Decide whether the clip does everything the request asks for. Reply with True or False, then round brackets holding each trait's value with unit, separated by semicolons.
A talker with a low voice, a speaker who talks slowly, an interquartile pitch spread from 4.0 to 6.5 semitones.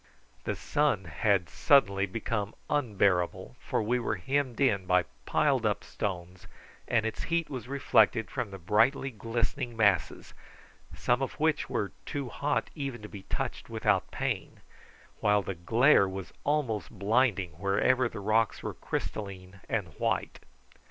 False (110 Hz; 145 wpm; 4.7 semitones)